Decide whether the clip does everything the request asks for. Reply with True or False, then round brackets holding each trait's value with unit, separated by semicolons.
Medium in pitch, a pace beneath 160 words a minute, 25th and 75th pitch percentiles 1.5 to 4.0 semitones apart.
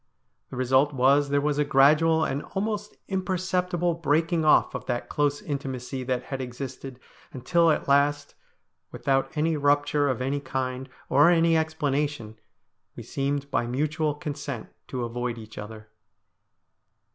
True (145 Hz; 140 wpm; 3.2 semitones)